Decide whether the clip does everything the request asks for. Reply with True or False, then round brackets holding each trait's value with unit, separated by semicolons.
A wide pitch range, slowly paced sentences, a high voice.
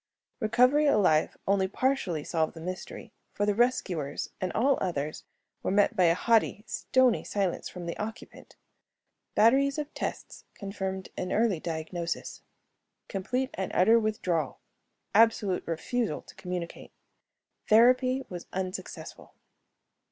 False (4.8 semitones; 120 wpm; 200 Hz)